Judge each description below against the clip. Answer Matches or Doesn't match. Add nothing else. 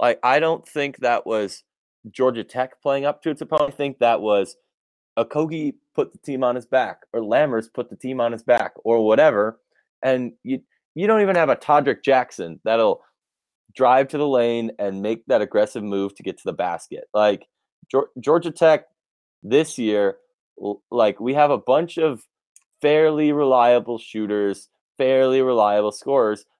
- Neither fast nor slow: Matches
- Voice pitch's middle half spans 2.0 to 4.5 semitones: Doesn't match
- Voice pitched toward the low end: Matches